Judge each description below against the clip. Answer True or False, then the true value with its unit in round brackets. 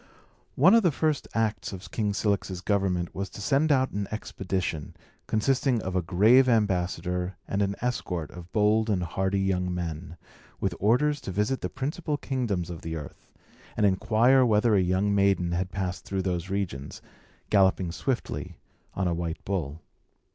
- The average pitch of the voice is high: False (100 Hz)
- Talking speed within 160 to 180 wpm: True (165 wpm)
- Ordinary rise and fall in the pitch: True (3.9 semitones)